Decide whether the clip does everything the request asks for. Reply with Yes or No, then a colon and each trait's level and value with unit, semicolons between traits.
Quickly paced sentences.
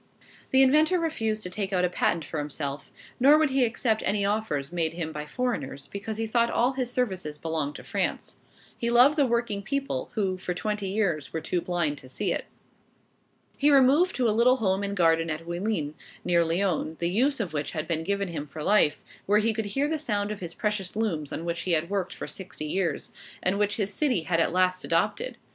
Yes: fast, 215 wpm